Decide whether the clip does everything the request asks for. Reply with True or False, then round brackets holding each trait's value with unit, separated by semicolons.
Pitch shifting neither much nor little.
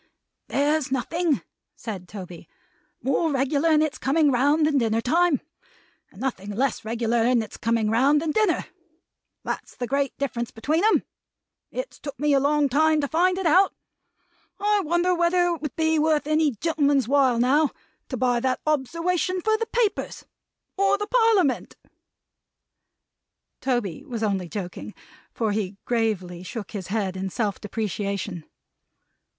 False (6.0 semitones)